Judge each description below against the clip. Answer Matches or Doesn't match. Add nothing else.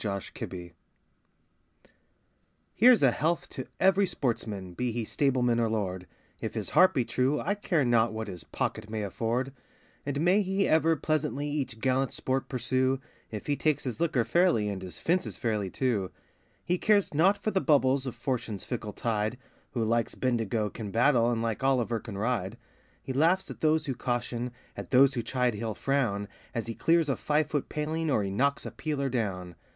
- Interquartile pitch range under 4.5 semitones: Doesn't match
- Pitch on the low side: Matches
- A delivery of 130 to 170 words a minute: Doesn't match